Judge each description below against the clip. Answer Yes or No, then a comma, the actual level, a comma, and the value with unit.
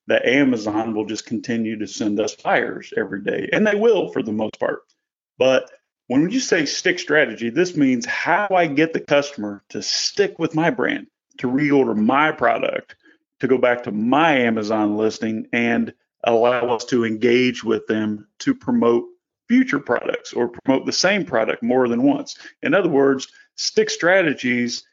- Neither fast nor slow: Yes, average, 170 wpm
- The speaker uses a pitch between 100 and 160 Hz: Yes, low, 135 Hz